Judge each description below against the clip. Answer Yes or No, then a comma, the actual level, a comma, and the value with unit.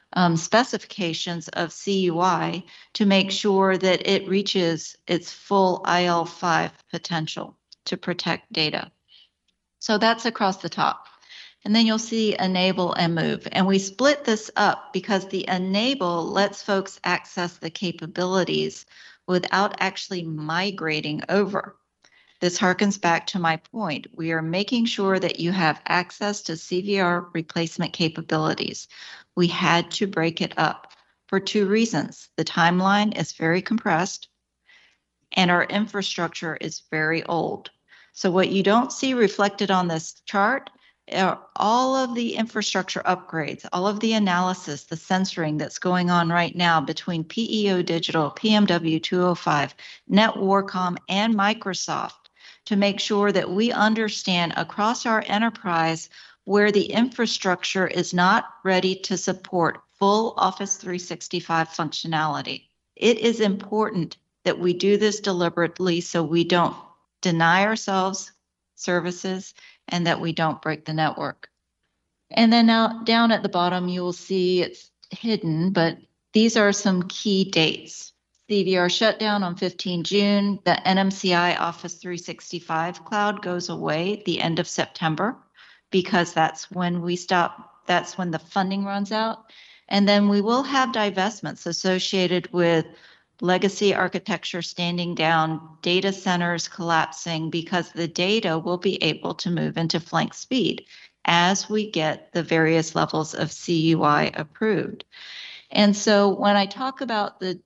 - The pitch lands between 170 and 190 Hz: Yes, medium, 185 Hz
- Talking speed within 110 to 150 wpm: Yes, average, 140 wpm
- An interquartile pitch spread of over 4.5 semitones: No, average, 3.1 semitones